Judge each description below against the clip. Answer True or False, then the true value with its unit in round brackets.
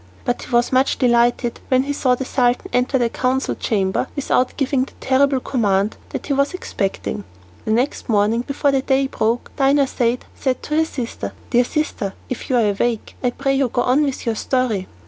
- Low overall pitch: False (255 Hz)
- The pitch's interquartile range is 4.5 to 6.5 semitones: False (2.4 semitones)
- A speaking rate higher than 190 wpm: True (200 wpm)